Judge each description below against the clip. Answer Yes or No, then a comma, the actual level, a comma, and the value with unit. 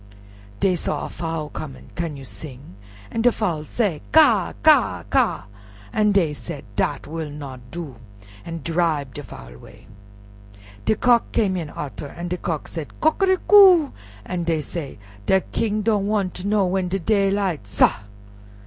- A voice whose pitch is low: No, medium, 170 Hz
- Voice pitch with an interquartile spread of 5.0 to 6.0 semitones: Yes, wide, 5.5 semitones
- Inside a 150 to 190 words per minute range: Yes, average, 160 wpm